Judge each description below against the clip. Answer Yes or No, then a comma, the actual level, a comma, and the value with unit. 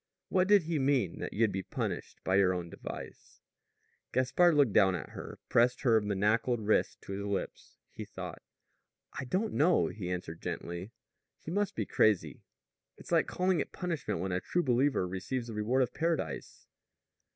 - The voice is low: Yes, low, 115 Hz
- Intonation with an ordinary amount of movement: No, wide, 7.6 semitones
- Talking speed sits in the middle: Yes, average, 175 wpm